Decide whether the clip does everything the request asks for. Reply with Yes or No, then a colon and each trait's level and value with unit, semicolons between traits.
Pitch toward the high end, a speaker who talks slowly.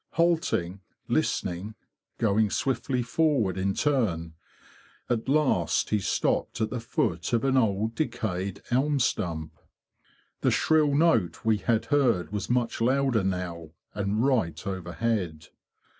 No: low, 110 Hz; slow, 130 wpm